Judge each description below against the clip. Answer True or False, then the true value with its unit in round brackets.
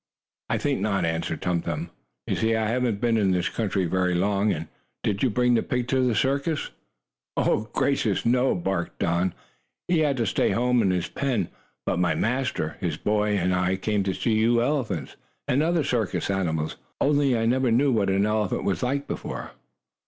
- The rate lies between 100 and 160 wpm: False (185 wpm)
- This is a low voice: True (105 Hz)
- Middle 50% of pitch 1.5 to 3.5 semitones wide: False (5.3 semitones)